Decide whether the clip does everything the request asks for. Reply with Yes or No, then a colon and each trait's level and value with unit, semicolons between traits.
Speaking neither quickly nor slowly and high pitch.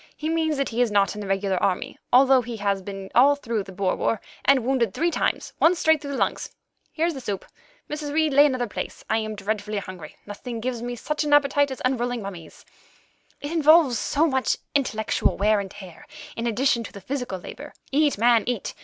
No: fast, 210 wpm; high, 245 Hz